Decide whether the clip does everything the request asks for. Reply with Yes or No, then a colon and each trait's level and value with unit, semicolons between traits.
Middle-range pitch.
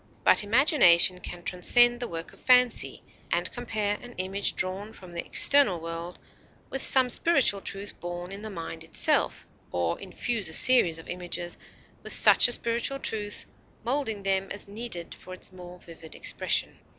No: high, 195 Hz